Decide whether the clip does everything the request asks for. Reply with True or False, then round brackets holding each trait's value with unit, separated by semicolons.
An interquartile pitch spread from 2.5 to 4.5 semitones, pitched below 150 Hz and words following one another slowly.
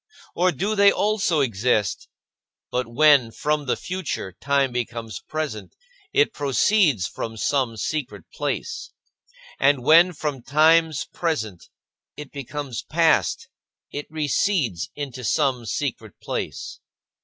False (5.1 semitones; 140 Hz; 115 wpm)